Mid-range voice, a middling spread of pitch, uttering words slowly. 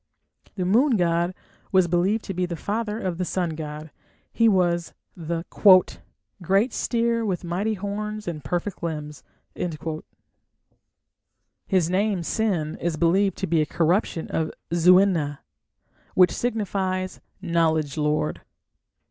Yes: medium, 180 Hz; average, 3.4 semitones; slow, 125 wpm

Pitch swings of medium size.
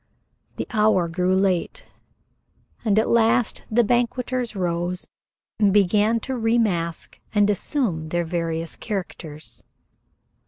Yes: average, 4.8 semitones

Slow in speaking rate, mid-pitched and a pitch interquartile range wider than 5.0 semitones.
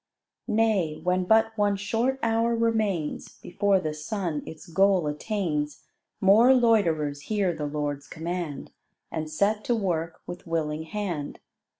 Yes: slow, 130 wpm; medium, 180 Hz; wide, 5.6 semitones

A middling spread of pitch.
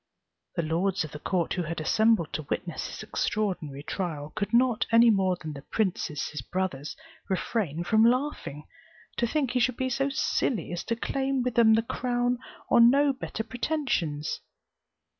No: wide, 6.6 semitones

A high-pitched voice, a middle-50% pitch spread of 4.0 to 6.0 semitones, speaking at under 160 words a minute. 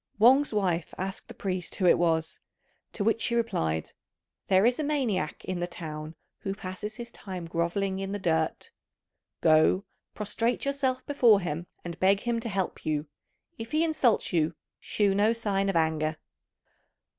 No: high, 195 Hz; average, 5.2 semitones; average, 165 wpm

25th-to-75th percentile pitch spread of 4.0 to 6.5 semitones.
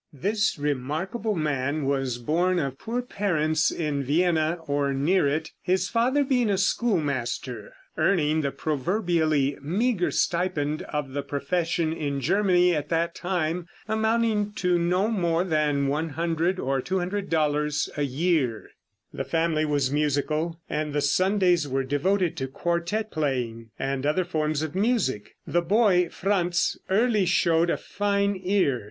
Yes: average, 4.4 semitones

